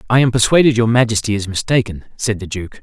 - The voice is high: No, low, 110 Hz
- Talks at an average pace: No, fast, 215 wpm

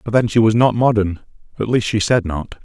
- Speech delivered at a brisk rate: Yes, fast, 250 wpm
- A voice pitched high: No, low, 110 Hz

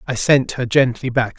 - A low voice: Yes, low, 125 Hz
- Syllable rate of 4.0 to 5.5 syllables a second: Yes, 4.9 syllables/s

